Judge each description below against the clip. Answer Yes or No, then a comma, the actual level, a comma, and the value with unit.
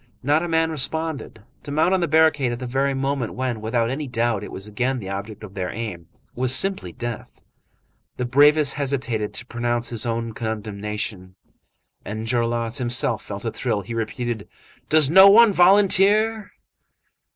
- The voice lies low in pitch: Yes, low, 120 Hz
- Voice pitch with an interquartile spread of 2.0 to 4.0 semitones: No, average, 5.3 semitones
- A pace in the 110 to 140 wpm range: No, average, 165 wpm